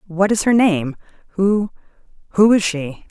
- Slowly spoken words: Yes, slow, 115 wpm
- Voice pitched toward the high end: Yes, high, 195 Hz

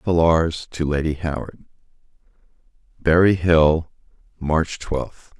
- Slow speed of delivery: Yes, slow, 90 wpm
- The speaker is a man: Yes, male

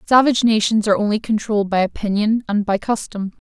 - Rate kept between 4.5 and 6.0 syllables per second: No, 6.3 syllables/s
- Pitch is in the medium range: No, high, 215 Hz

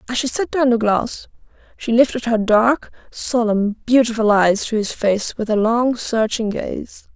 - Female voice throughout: Yes, female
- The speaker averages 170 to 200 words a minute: Yes, average, 175 wpm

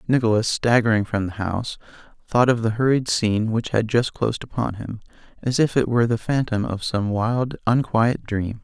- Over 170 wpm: Yes, average, 190 wpm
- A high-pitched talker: No, low, 115 Hz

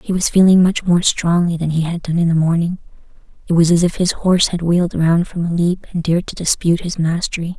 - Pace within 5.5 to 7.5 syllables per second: Yes, 6.0 syllables/s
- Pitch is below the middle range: No, medium, 170 Hz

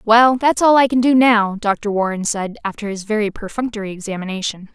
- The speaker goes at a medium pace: Yes, average, 190 wpm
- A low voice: No, high, 215 Hz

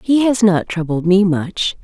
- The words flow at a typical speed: Yes, average, 195 wpm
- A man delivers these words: No, female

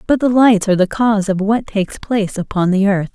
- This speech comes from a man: No, female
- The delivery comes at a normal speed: No, fast, 250 wpm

